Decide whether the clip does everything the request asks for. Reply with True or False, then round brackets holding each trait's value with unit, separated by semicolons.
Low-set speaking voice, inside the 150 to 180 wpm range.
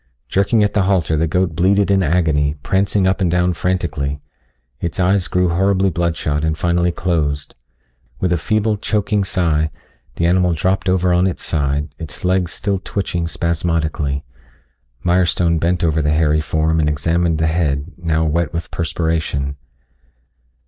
True (85 Hz; 155 wpm)